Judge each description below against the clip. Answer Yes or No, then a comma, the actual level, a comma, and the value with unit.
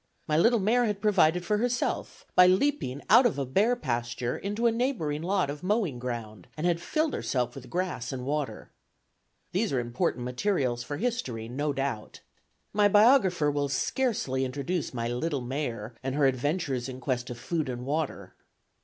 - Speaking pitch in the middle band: Yes, medium, 145 Hz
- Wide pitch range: Yes, wide, 8.0 semitones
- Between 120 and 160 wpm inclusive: No, average, 170 wpm